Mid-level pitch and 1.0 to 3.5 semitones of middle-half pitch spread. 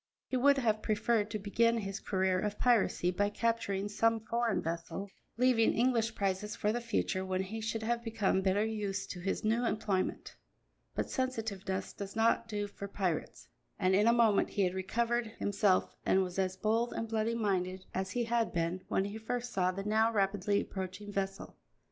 No: high, 210 Hz; average, 3.0 semitones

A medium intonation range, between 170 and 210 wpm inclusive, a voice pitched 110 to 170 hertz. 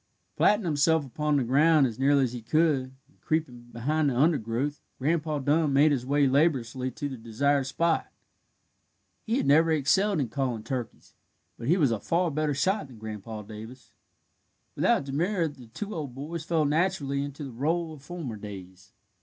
Yes: average, 4.1 semitones; average, 175 wpm; medium, 140 Hz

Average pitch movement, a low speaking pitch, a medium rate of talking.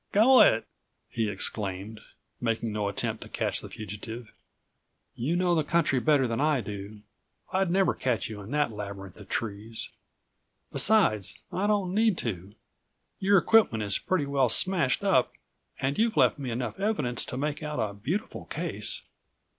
No: wide, 8.3 semitones; low, 125 Hz; average, 160 wpm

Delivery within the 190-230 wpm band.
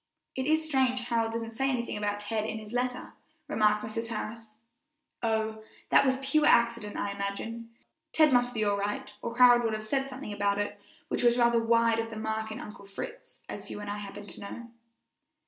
Yes: average, 200 wpm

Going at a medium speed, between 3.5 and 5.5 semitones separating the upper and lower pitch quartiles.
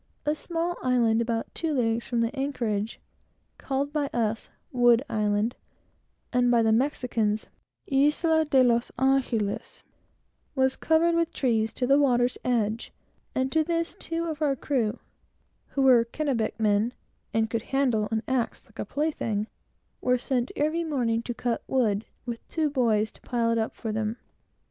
Yes: average, 160 wpm; average, 3.8 semitones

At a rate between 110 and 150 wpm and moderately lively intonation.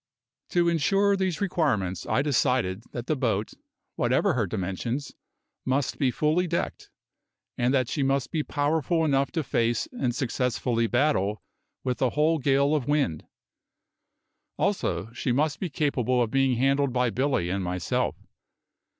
Yes: average, 145 wpm; average, 4.2 semitones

